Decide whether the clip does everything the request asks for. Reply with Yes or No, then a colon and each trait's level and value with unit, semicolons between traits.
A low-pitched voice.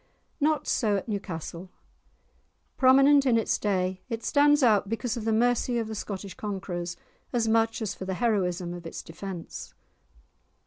No: high, 215 Hz